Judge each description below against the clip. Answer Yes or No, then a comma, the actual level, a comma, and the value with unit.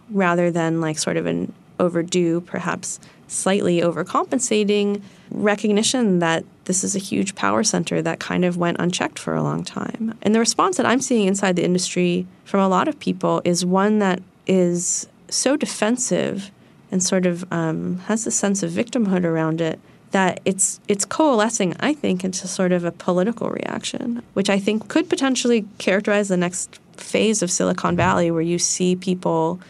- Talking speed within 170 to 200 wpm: Yes, average, 175 wpm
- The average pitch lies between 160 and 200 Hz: Yes, high, 190 Hz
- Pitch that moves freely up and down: No, average, 3.3 semitones